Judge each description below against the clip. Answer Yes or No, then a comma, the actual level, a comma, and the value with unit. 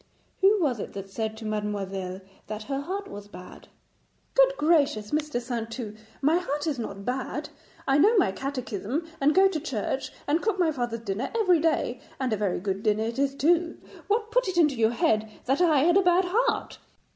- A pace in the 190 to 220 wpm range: Yes, average, 195 wpm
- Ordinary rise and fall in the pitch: No, wide, 7.9 semitones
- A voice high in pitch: Yes, very high, 270 Hz